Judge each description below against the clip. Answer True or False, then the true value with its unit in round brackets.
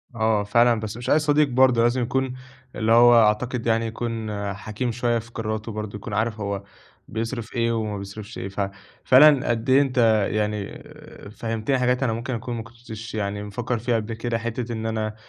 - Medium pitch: False (115 Hz)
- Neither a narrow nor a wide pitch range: False (2.1 semitones)